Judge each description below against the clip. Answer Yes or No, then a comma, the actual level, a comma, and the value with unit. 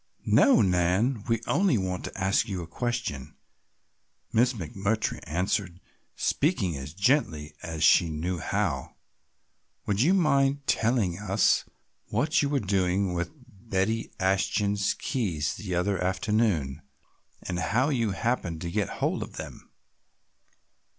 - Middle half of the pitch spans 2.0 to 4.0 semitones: No, average, 4.9 semitones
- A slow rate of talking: Yes, slow, 130 wpm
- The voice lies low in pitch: Yes, low, 100 Hz